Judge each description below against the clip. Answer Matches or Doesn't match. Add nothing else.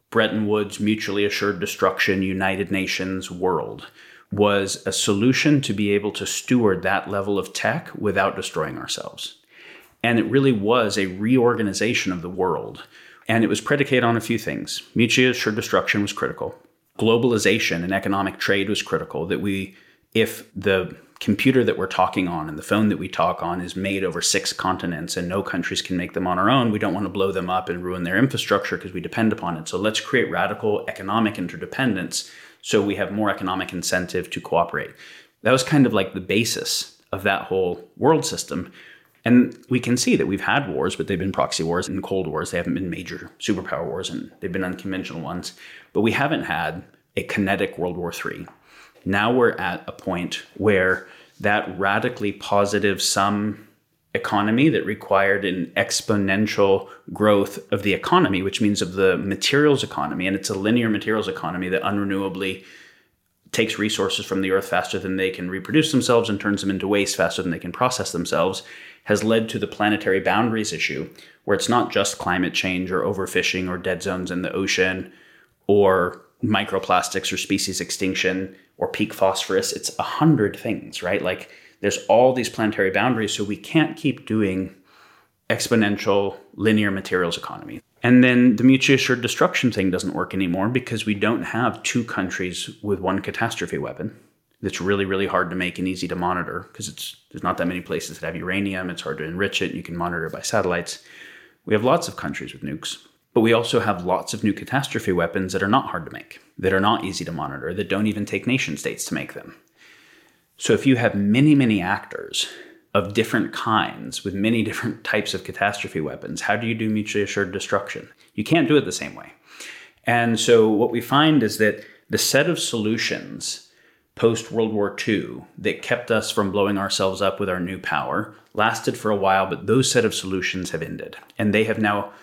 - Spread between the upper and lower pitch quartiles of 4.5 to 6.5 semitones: Doesn't match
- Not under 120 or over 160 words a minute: Doesn't match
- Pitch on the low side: Matches